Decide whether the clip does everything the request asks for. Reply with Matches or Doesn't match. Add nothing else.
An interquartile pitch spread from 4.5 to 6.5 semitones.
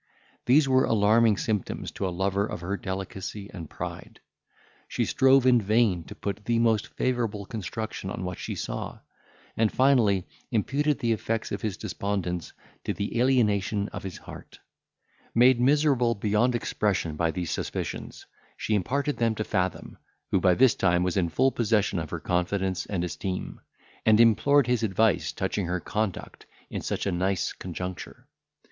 Doesn't match